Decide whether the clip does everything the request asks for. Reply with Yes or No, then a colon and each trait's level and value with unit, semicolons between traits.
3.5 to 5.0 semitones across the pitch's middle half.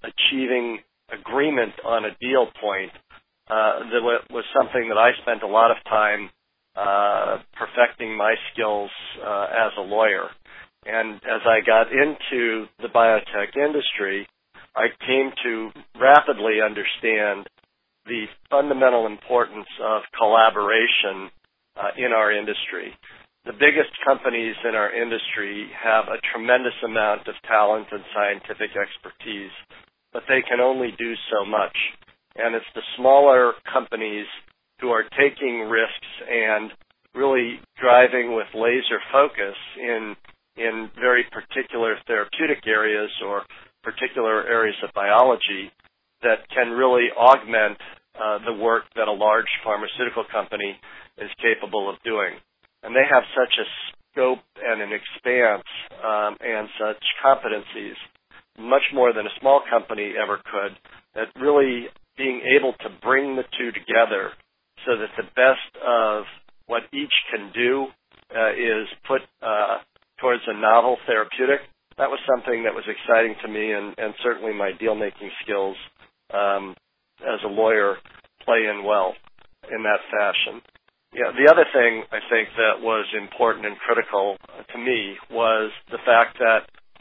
No: average, 2.7 semitones